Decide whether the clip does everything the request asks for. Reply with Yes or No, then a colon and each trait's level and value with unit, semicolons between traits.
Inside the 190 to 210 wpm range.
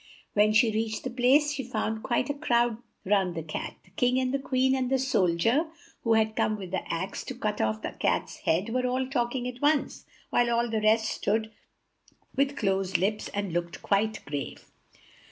Yes: average, 200 wpm